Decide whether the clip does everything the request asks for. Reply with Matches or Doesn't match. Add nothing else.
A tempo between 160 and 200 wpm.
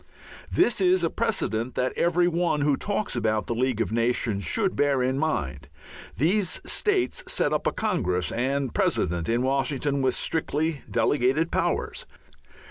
Doesn't match